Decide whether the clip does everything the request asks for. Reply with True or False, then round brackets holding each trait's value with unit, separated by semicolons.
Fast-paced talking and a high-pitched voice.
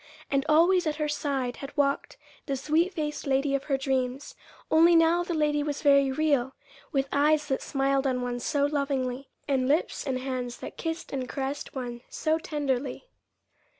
False (175 wpm; 280 Hz)